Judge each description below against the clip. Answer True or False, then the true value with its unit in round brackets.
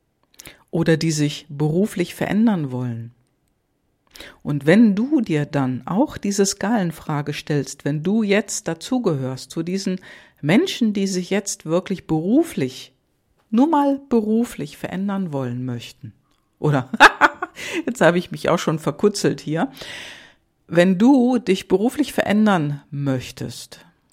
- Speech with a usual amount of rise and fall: False (6.9 semitones)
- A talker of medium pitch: True (175 Hz)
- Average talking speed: False (120 wpm)